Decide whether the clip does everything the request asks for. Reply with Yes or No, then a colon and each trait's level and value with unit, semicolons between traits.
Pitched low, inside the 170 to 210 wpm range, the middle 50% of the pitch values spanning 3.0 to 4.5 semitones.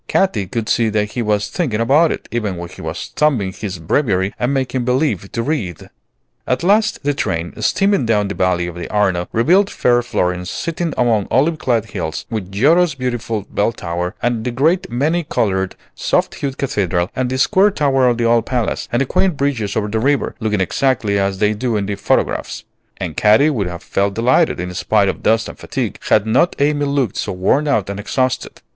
No: low, 115 Hz; average, 200 wpm; wide, 5.6 semitones